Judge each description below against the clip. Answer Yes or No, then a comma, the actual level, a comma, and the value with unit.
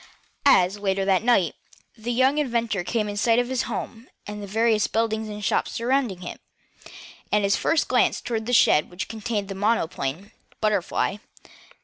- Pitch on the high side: Yes, high, 215 Hz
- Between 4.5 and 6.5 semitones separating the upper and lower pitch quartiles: No, average, 3.0 semitones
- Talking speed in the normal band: Yes, average, 165 wpm